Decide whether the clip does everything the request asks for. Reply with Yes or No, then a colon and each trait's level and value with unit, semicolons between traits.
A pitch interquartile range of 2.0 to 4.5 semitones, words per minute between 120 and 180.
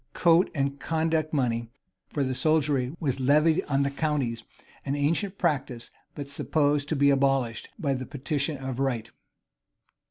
Yes: average, 2.7 semitones; average, 150 wpm